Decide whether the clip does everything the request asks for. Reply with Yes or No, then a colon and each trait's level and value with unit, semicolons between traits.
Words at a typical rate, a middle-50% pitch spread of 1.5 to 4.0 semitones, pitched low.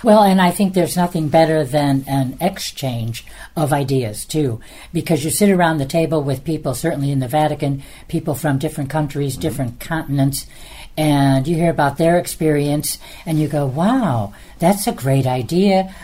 No: average, 170 wpm; average, 3.3 semitones; medium, 155 Hz